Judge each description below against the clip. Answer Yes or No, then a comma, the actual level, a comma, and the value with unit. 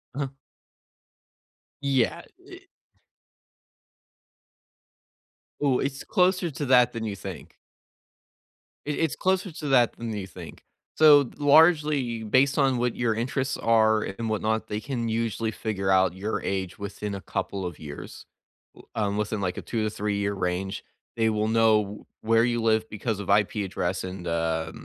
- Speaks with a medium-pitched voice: No, low, 110 Hz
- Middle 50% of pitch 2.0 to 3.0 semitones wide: No, average, 4.5 semitones